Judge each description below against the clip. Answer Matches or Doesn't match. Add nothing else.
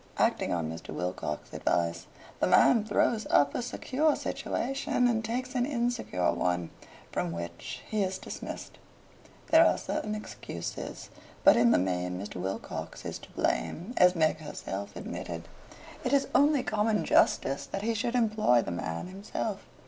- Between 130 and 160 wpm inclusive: Matches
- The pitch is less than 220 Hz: Matches